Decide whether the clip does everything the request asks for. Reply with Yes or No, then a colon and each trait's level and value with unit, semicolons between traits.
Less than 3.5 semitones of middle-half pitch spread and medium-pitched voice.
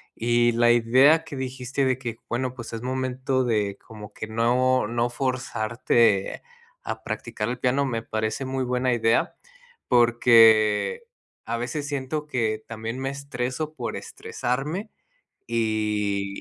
No: narrow, 2.5 semitones; low, 120 Hz